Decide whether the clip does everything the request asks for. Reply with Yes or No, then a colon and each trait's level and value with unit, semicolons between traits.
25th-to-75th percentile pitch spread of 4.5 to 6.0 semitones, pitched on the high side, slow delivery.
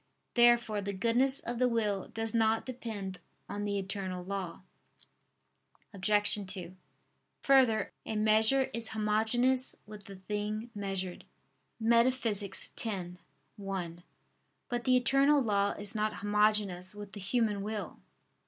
No: average, 2.8 semitones; high, 210 Hz; slow, 125 wpm